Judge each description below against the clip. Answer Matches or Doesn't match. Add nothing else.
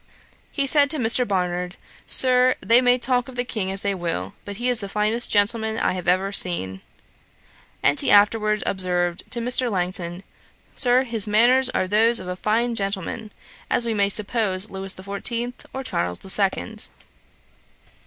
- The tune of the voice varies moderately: Matches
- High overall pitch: Matches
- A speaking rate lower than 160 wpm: Doesn't match